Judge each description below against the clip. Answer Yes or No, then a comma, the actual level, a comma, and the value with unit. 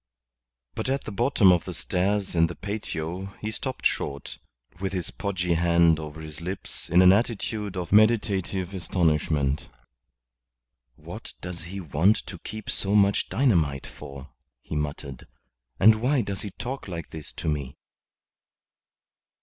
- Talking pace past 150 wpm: No, average, 145 wpm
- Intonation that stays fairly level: No, average, 4.3 semitones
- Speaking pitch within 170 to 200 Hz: No, very low, 90 Hz